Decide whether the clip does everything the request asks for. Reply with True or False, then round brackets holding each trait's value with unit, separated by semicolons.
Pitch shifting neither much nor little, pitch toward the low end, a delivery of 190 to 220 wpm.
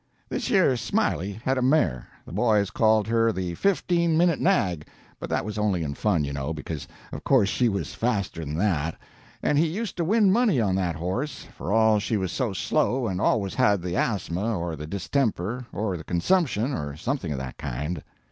False (6.9 semitones; 105 Hz; 200 wpm)